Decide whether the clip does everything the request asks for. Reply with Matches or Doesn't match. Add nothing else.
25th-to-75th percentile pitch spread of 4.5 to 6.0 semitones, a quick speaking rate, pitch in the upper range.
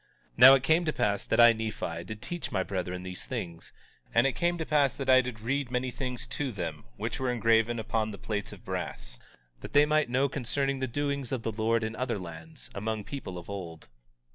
Doesn't match